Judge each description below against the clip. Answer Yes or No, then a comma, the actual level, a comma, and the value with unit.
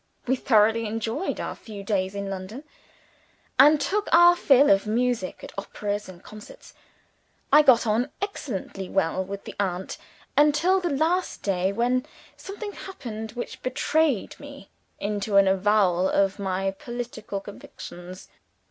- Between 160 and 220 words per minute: No, average, 140 wpm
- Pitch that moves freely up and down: Yes, wide, 6.1 semitones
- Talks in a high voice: Yes, high, 220 Hz